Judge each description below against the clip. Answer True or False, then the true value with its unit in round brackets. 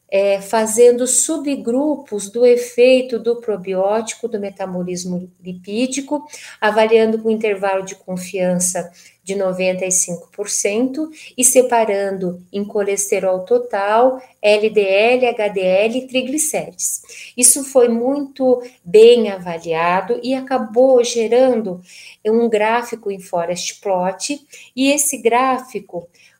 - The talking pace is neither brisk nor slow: False (100 wpm)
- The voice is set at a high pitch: True (220 Hz)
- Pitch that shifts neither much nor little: True (4.6 semitones)